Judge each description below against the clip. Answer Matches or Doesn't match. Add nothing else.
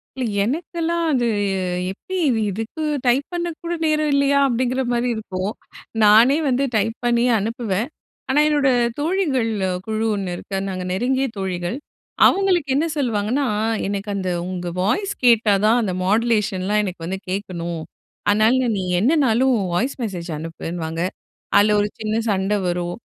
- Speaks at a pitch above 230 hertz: Doesn't match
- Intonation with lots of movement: Matches